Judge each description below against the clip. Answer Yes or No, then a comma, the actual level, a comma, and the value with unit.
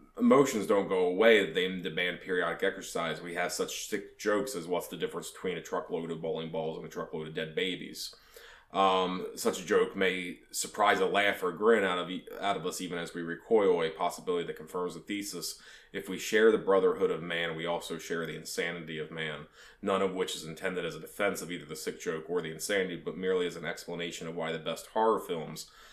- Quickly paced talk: Yes, fast, 220 wpm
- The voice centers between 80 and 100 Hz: Yes, very low, 95 Hz